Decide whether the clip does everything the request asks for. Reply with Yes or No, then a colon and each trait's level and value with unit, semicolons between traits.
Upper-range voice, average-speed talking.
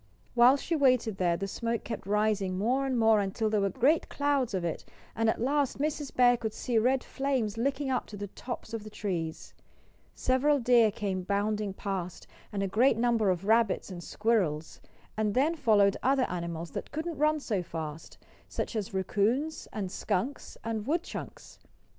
Yes: high, 220 Hz; average, 175 wpm